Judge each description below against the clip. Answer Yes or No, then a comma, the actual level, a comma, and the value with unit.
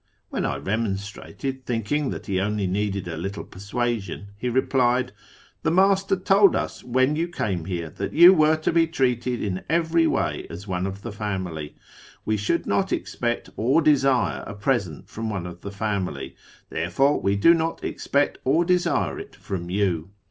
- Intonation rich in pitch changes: Yes, wide, 7.3 semitones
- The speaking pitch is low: Yes, low, 115 Hz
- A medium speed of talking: Yes, average, 175 wpm